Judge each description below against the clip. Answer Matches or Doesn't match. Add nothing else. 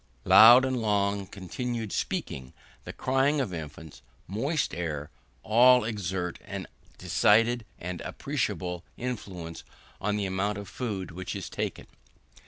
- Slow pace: Matches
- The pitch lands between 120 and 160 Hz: Doesn't match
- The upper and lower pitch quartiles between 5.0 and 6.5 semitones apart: Matches